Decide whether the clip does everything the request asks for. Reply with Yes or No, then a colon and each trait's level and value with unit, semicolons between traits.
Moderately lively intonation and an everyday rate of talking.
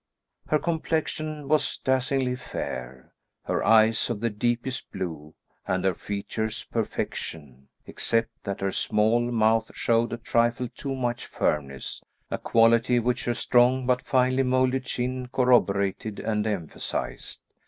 No: average, 3.4 semitones; slow, 130 wpm